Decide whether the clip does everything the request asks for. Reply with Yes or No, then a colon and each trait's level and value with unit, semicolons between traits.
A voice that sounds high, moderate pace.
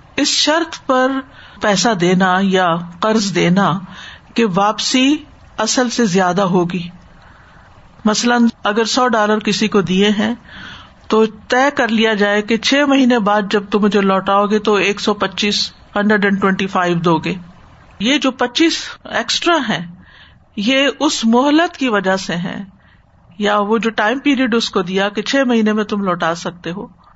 Yes: high, 215 Hz; average, 160 wpm